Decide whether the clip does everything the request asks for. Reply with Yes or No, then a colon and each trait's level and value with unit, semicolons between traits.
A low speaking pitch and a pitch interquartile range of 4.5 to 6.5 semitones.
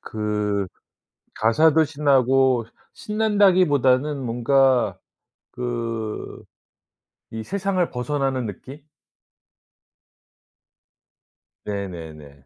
Yes: low, 130 Hz; average, 5.3 semitones